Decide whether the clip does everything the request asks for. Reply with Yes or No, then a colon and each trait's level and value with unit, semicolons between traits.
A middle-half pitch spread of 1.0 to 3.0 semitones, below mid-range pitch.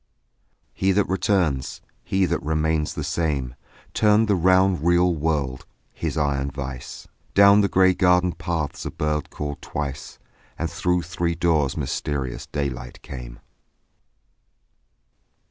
No: average, 4.3 semitones; very low, 80 Hz